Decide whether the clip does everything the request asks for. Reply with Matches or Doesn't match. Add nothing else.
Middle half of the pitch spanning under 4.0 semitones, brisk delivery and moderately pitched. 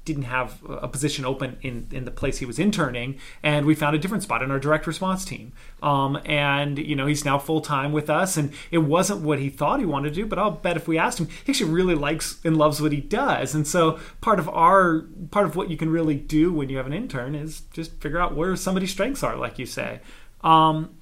Matches